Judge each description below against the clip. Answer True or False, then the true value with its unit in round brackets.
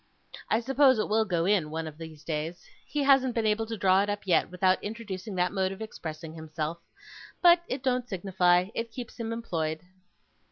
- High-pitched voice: True (195 Hz)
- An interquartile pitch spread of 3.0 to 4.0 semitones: False (5.4 semitones)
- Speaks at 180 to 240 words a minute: True (195 wpm)